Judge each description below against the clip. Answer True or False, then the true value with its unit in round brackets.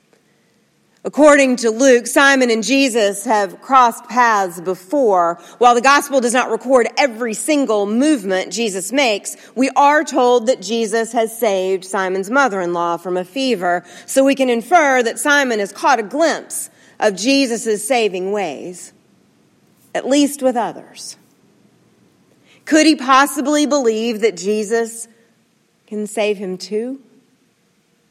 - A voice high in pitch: True (230 Hz)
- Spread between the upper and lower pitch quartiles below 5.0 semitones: True (4.3 semitones)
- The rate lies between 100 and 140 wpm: True (135 wpm)